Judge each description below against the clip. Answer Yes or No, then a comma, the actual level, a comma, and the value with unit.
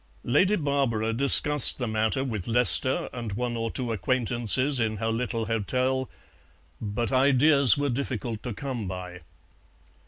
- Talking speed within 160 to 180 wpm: No, slow, 135 wpm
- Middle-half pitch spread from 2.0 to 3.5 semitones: Yes, average, 3.0 semitones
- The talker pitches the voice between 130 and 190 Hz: No, low, 120 Hz